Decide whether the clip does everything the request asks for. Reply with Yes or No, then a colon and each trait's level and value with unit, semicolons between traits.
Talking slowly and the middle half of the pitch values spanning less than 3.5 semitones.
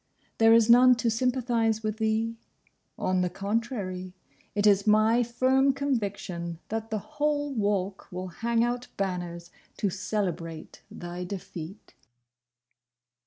No: slow, 120 wpm; average, 4.2 semitones